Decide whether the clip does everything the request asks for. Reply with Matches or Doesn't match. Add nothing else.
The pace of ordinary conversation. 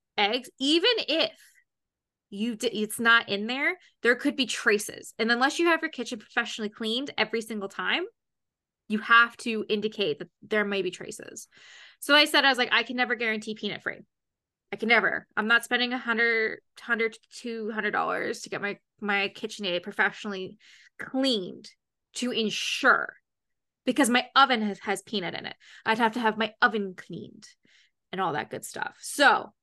Matches